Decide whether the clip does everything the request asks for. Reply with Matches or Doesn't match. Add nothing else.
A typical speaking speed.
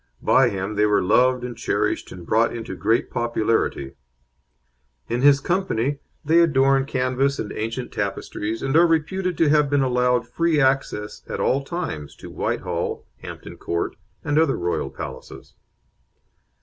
Matches